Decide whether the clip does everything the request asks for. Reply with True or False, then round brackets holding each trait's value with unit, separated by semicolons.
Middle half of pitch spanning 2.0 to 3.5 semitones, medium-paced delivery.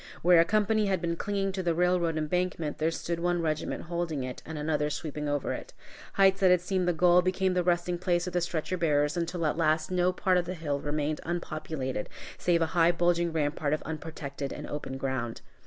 False (2.7 semitones; 210 wpm)